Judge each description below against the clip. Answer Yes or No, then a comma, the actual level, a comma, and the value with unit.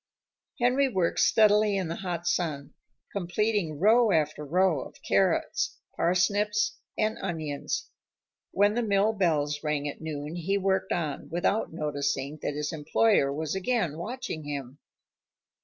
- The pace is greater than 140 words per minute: No, slow, 135 wpm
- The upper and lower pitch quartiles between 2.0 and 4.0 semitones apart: No, wide, 5.6 semitones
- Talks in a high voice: No, medium, 175 Hz